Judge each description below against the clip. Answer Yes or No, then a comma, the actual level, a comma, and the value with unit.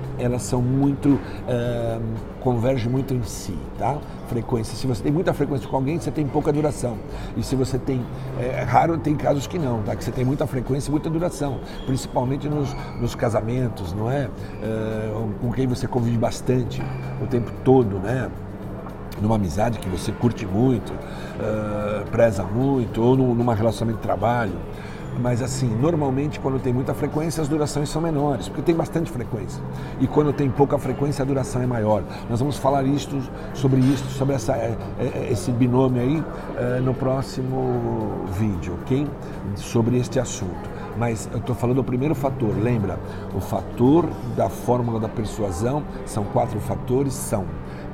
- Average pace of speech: Yes, average, 165 wpm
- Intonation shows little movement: No, average, 3.7 semitones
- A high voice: No, low, 125 Hz